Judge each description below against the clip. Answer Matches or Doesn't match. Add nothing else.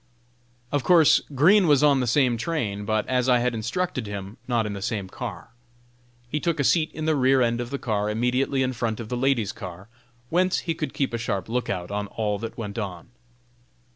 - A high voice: Doesn't match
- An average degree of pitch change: Matches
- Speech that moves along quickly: Matches